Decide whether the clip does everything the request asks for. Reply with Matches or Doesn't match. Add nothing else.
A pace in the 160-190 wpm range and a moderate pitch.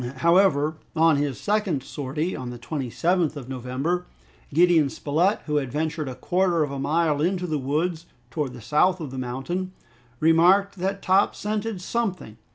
Matches